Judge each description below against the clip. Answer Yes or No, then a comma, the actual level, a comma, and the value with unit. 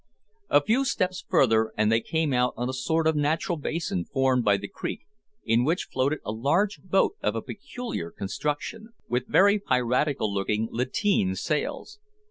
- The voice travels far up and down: Yes, wide, 6.7 semitones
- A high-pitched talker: No, low, 135 Hz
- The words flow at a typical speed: Yes, average, 165 wpm